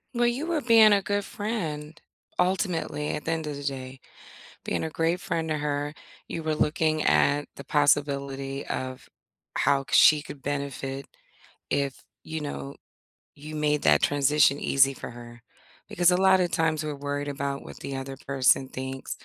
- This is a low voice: No, medium, 145 Hz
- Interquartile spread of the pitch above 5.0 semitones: No, average, 2.8 semitones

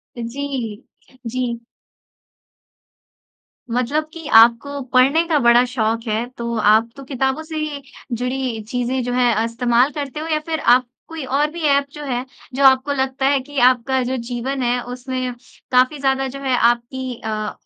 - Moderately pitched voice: No, very high, 255 Hz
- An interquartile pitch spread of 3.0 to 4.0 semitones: No, narrow, 2.6 semitones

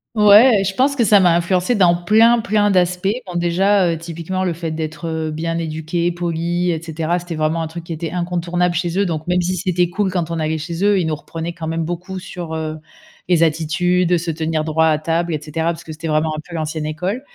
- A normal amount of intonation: No, narrow, 2.1 semitones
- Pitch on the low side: No, medium, 170 Hz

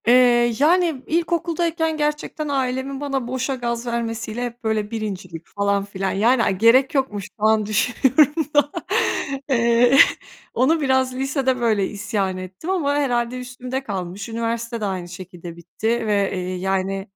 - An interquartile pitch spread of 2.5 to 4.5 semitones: No, average, 4.9 semitones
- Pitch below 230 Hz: No, high, 235 Hz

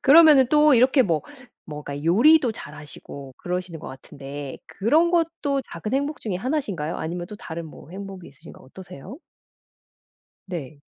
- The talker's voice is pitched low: No, medium, 185 Hz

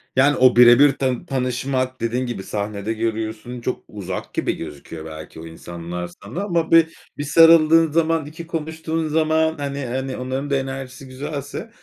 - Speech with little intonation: No, average, 5.2 semitones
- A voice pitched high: No, low, 130 Hz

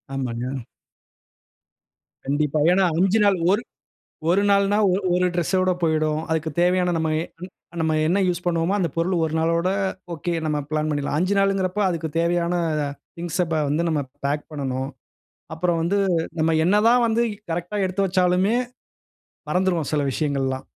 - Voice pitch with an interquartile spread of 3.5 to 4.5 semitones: No, average, 3.1 semitones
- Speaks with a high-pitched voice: No, medium, 170 Hz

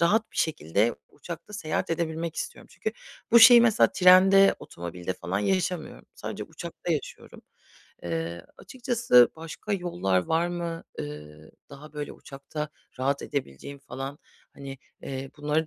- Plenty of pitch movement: Yes, wide, 6.9 semitones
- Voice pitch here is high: No, medium, 150 Hz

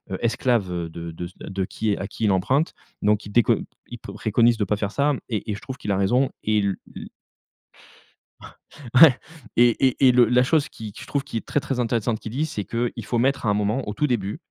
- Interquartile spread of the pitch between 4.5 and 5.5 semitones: No, average, 3.7 semitones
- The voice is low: Yes, low, 115 Hz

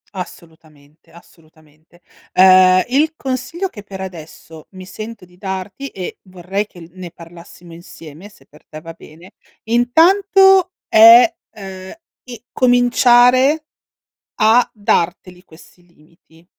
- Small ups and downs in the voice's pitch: No, wide, 6.3 semitones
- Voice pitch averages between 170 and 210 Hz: Yes, high, 190 Hz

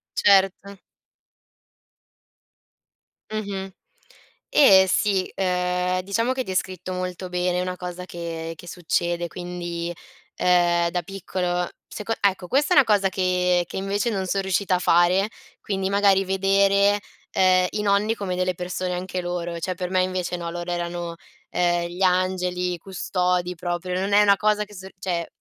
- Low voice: No, medium, 185 Hz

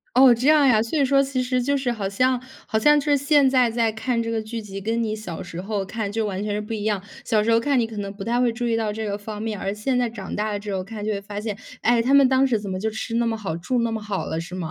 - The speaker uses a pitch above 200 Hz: Yes, high, 225 Hz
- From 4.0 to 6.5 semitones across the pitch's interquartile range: No, average, 3.2 semitones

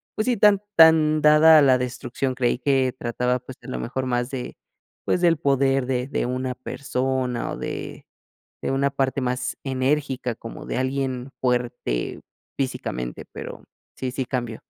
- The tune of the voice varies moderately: No, narrow, 1.8 semitones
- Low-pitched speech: Yes, low, 130 Hz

